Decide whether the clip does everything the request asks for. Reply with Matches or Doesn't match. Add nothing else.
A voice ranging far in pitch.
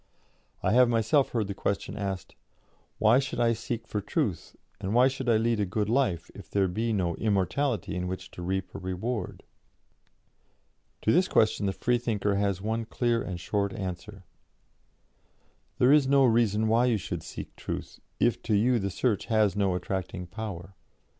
Doesn't match